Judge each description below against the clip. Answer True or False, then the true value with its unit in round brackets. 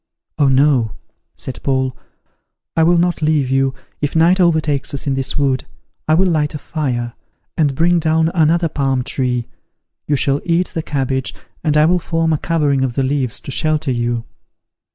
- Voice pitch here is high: False (145 Hz)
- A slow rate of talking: False (175 wpm)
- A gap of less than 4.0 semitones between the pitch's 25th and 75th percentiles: True (3.4 semitones)